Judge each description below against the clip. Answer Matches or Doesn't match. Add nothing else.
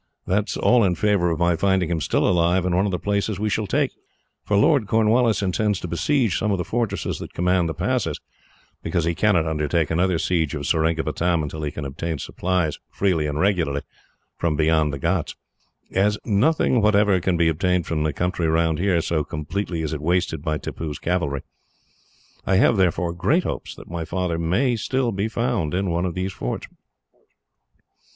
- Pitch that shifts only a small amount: Doesn't match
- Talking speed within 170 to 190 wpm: Matches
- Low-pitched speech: Matches